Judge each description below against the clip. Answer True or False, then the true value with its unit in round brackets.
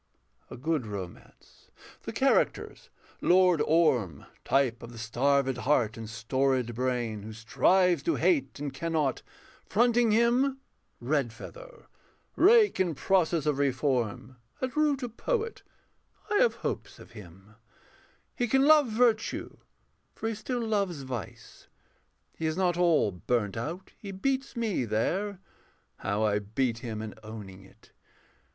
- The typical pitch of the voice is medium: True (145 Hz)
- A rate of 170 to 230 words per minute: False (135 wpm)